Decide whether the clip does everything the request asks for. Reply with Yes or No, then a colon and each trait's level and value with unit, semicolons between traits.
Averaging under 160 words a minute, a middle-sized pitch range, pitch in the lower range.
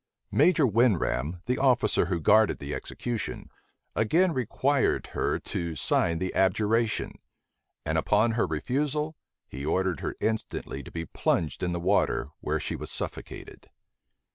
No: average, 140 wpm; wide, 6.7 semitones; low, 105 Hz